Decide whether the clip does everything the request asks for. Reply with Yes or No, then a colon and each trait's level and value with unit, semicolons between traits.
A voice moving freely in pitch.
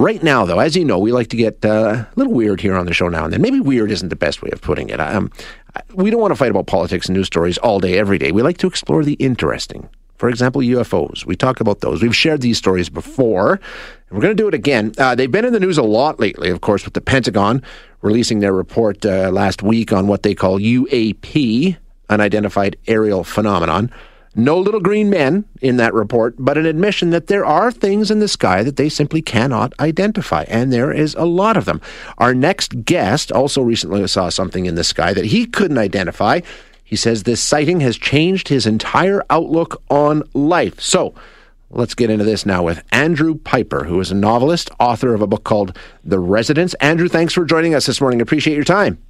Yes: wide, 7.6 semitones